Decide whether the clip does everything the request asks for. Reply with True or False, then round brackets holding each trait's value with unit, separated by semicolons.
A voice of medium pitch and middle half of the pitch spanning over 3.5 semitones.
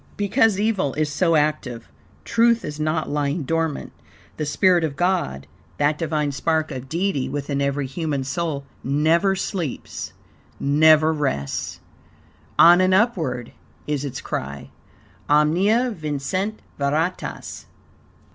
True (155 Hz; 4.1 semitones)